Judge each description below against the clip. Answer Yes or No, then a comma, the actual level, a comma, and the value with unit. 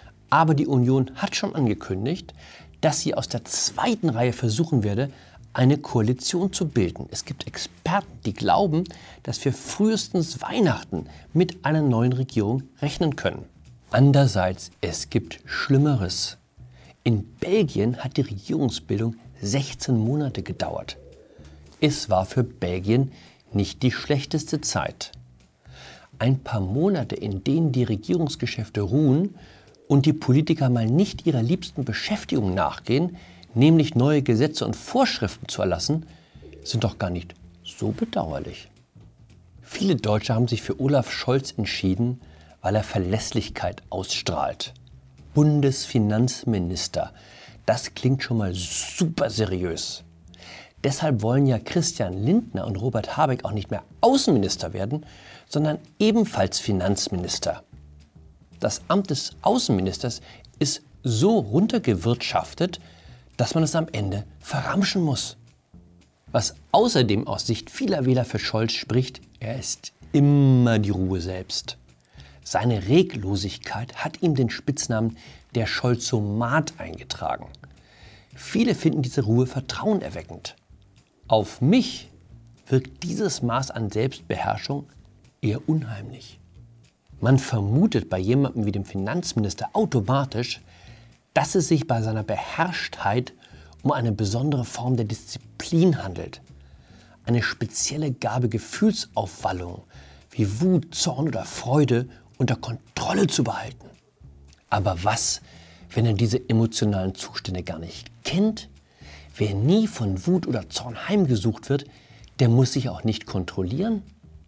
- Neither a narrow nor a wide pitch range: No, wide, 6.3 semitones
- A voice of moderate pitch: No, low, 120 Hz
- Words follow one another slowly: Yes, slow, 120 wpm